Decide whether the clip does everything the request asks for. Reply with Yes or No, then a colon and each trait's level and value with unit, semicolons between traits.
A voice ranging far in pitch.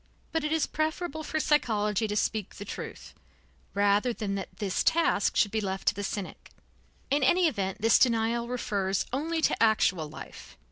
Yes: wide, 6.7 semitones